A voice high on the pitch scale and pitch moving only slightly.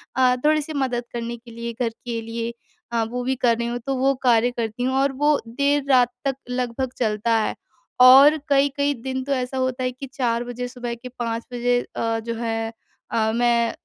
Yes: high, 245 Hz; narrow, 2.1 semitones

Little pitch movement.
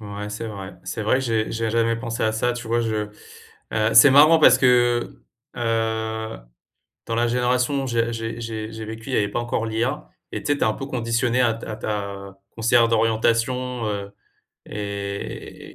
Yes: narrow, 1.7 semitones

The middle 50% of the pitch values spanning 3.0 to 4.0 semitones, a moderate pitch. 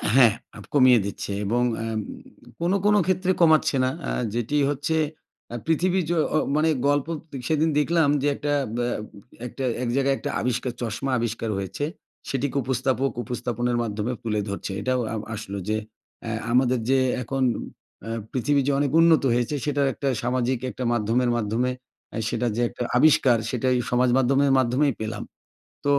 No: average, 3.3 semitones; low, 130 Hz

